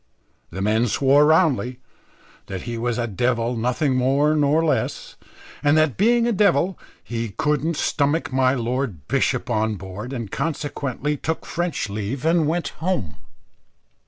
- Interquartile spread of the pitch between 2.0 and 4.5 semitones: No, average, 5.2 semitones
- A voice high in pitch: No, low, 135 Hz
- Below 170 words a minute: Yes, average, 145 wpm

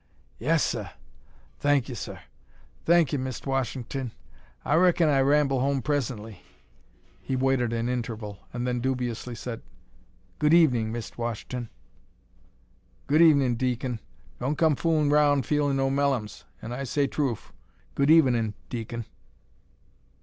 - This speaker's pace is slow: Yes, slow, 130 wpm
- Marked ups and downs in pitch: No, average, 3.4 semitones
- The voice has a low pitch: Yes, low, 130 Hz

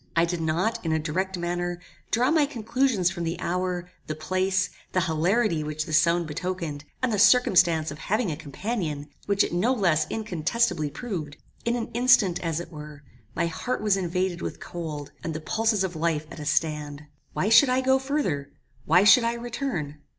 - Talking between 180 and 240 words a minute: Yes, average, 185 wpm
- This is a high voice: No, medium, 175 Hz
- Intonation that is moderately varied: No, wide, 5.8 semitones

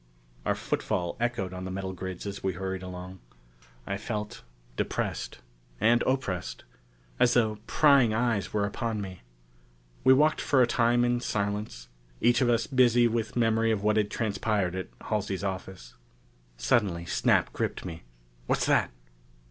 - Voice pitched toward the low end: Yes, low, 105 Hz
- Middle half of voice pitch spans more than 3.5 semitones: Yes, average, 4.2 semitones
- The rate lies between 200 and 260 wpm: No, average, 150 wpm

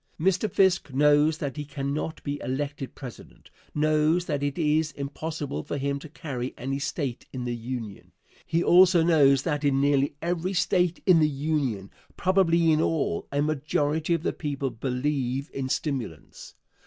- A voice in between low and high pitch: Yes, medium, 145 Hz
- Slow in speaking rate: No, average, 160 wpm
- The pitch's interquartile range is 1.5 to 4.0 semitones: Yes, average, 2.9 semitones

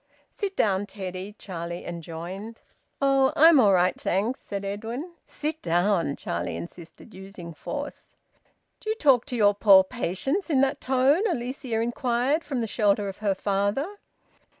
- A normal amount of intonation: No, wide, 6.2 semitones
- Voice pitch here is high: Yes, high, 215 Hz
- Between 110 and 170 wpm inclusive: Yes, average, 150 wpm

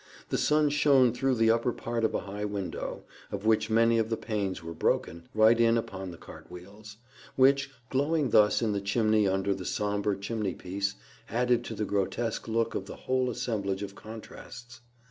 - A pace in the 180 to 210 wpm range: Yes, average, 185 wpm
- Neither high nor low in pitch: No, low, 110 Hz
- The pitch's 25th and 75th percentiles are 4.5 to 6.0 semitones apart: No, average, 2.9 semitones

